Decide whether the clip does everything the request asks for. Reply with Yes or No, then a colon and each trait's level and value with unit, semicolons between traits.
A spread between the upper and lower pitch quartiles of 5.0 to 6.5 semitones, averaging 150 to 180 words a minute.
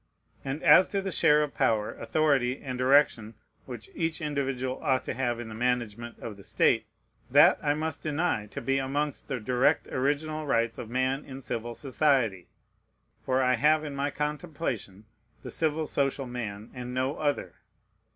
No: average, 3.7 semitones; average, 170 wpm